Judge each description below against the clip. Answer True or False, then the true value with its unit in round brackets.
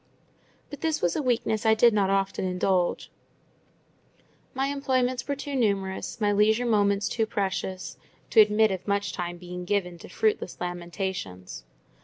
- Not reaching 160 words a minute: True (150 wpm)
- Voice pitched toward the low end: False (200 Hz)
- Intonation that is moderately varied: True (3.9 semitones)